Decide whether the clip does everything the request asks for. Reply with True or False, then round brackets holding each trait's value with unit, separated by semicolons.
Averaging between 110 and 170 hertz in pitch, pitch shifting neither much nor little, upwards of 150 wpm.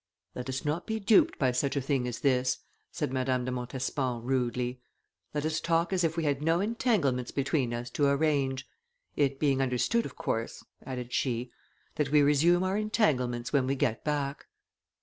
True (135 Hz; 3.8 semitones; 180 wpm)